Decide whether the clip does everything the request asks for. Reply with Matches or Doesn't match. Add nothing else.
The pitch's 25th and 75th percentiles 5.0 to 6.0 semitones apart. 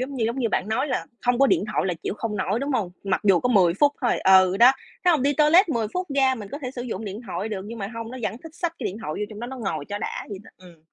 Matches